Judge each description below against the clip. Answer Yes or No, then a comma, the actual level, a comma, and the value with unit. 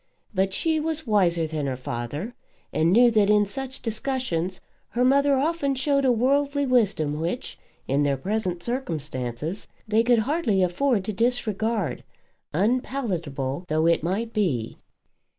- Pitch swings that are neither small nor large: No, wide, 7.5 semitones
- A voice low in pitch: No, high, 210 Hz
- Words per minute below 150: Yes, average, 140 wpm